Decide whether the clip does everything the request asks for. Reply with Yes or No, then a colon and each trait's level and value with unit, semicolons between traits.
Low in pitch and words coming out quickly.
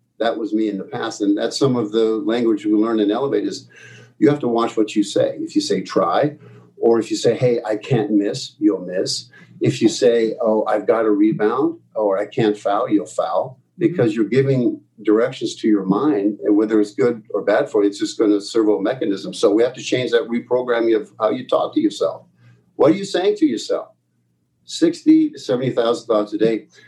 Yes: low, 115 Hz; fast, 220 wpm